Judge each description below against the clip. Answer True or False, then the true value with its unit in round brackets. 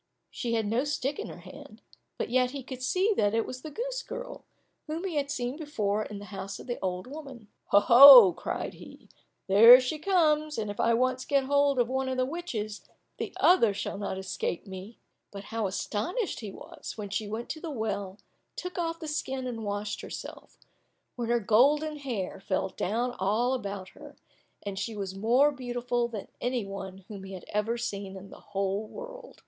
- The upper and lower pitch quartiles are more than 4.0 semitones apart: True (5.6 semitones)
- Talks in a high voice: True (235 Hz)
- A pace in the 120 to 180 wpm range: False (195 wpm)